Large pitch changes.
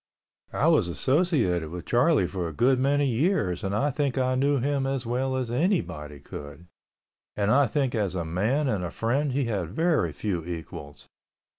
Yes: wide, 7.8 semitones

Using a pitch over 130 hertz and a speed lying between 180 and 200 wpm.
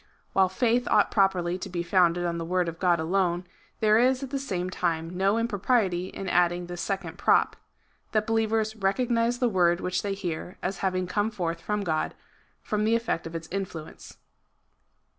Yes: high, 190 Hz; average, 190 wpm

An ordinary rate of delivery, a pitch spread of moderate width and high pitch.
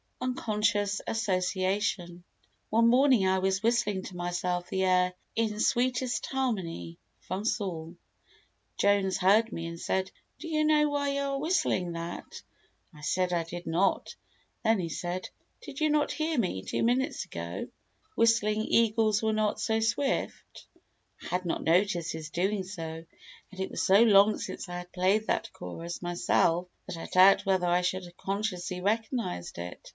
Yes: average, 160 wpm; average, 4.2 semitones; high, 195 Hz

